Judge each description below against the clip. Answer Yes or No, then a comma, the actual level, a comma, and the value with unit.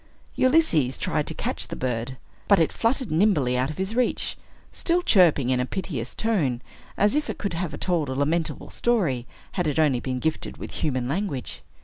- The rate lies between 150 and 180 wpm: No, average, 190 wpm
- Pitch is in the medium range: Yes, medium, 155 Hz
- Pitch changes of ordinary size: No, wide, 7.6 semitones